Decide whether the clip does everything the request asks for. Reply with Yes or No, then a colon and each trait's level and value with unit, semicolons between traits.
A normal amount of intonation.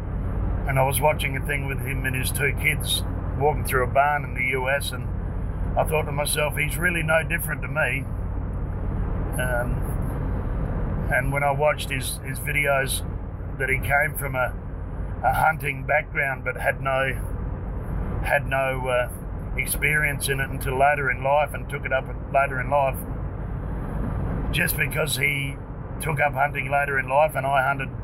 No: wide, 6.0 semitones